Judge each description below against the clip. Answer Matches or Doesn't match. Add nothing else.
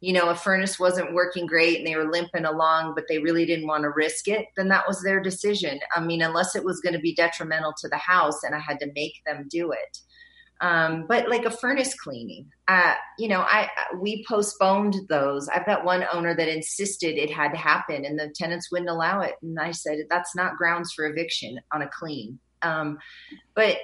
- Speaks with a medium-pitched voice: Matches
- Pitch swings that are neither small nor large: Matches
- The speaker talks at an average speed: Doesn't match